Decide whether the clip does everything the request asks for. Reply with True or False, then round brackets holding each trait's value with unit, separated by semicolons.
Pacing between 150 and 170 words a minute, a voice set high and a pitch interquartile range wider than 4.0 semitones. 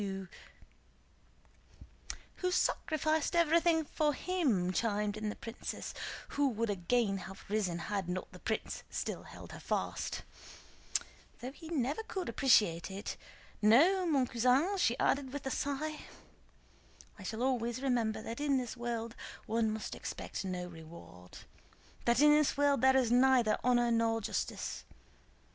False (140 wpm; 240 Hz; 5.1 semitones)